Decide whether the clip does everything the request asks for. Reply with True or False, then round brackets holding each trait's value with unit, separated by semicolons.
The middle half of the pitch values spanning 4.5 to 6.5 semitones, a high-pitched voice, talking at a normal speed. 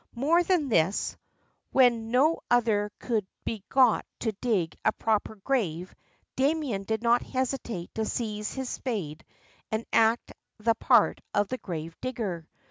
False (3.8 semitones; 225 Hz; 145 wpm)